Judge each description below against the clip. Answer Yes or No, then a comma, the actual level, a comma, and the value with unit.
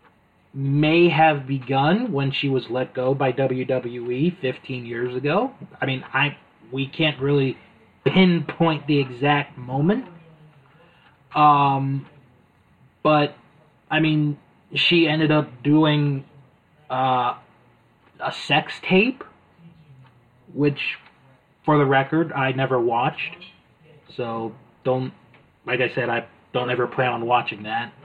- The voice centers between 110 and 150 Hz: Yes, medium, 140 Hz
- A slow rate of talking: Yes, slow, 115 wpm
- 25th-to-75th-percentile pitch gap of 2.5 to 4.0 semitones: Yes, average, 3.1 semitones